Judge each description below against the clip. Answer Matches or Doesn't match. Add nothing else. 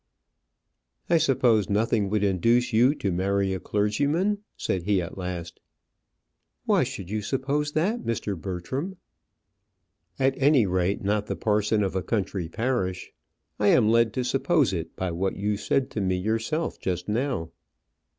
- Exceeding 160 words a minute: Doesn't match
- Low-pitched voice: Matches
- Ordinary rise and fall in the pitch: Doesn't match